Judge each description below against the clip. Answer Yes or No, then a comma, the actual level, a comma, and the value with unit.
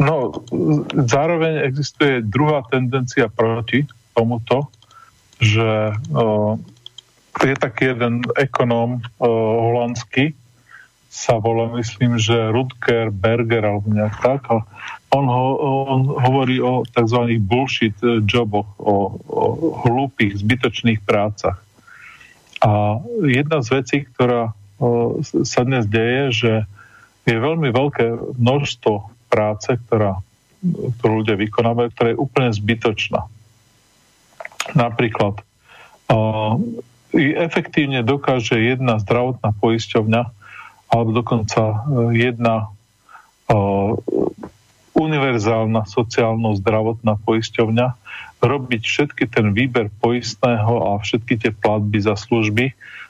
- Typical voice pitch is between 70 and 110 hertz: No, low, 120 Hz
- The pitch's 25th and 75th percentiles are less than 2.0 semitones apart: No, narrow, 2.5 semitones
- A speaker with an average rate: No, slow, 95 wpm